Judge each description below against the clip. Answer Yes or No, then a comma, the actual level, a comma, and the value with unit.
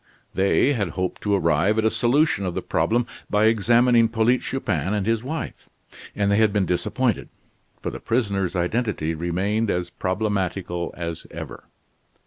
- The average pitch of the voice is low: Yes, low, 105 Hz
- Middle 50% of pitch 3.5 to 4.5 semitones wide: Yes, average, 4.0 semitones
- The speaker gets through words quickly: No, average, 155 wpm